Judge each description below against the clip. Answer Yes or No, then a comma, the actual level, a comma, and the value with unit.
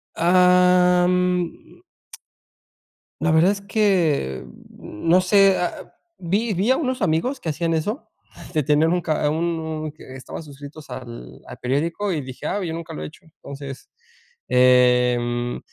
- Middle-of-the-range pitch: Yes, medium, 165 Hz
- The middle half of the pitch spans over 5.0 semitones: No, average, 4.7 semitones